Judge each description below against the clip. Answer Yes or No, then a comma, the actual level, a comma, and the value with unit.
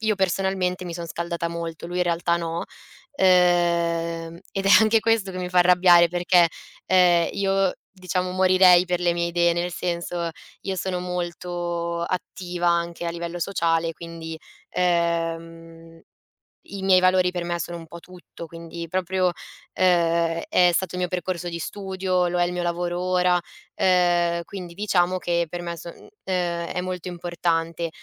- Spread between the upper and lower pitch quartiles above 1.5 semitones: No, narrow, 1.2 semitones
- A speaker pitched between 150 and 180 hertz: Yes, medium, 175 Hz